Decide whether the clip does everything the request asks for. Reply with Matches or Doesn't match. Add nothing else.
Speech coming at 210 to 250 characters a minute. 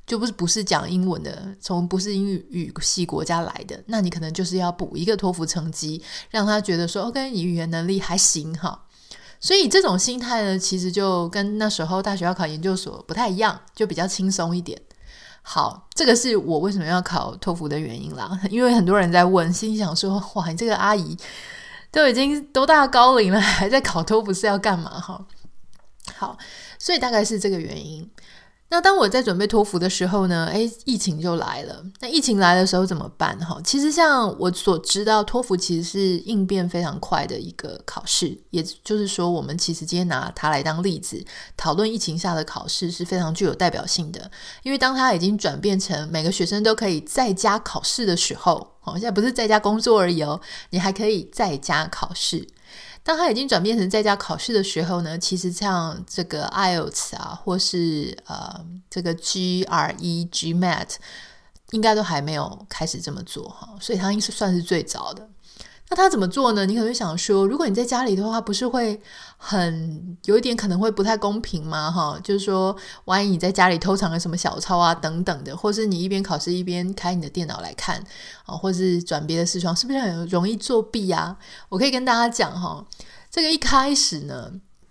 Doesn't match